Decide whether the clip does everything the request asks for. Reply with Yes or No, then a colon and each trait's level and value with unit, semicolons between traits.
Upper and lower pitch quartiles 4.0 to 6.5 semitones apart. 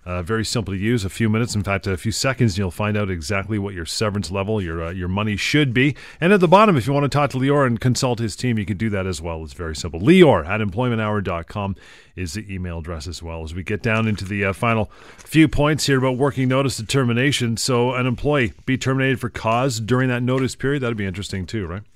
Yes: average, 5.0 semitones